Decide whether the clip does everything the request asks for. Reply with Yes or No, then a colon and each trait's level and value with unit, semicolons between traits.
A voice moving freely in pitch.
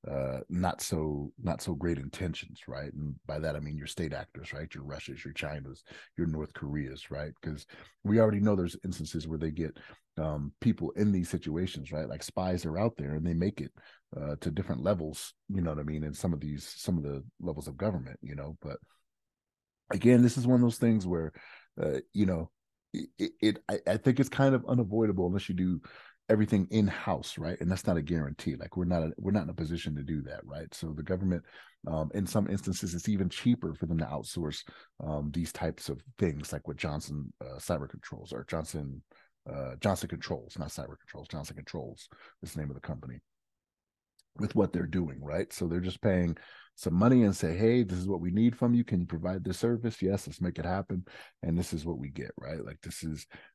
No: average, 4.4 semitones